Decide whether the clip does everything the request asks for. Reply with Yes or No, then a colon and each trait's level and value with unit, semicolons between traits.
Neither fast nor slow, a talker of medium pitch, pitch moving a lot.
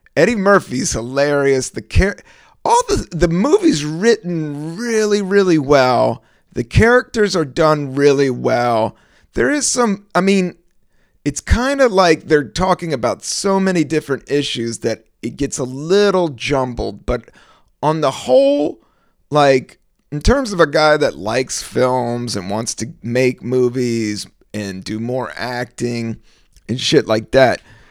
Yes: average, 145 wpm; medium, 145 Hz; wide, 7.9 semitones